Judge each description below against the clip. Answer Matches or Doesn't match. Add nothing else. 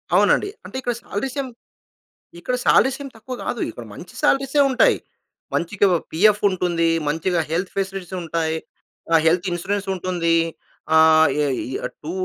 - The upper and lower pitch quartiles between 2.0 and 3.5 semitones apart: Doesn't match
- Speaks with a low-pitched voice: Doesn't match